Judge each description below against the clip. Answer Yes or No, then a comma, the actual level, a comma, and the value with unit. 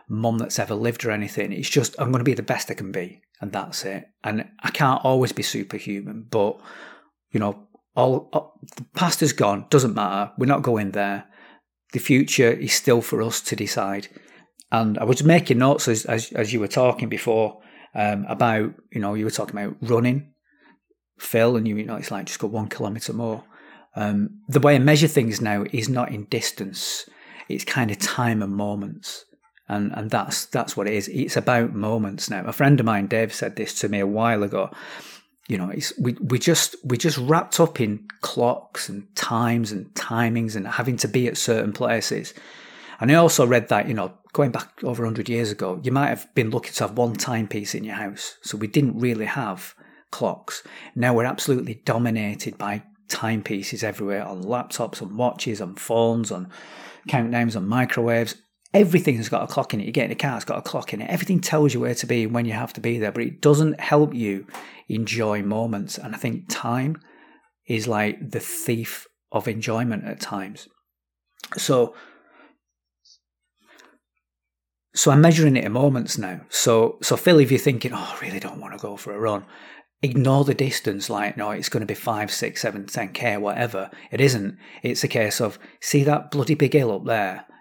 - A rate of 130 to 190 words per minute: No, average, 200 wpm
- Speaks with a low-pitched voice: Yes, low, 115 Hz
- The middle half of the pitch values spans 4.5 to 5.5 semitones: No, average, 4.0 semitones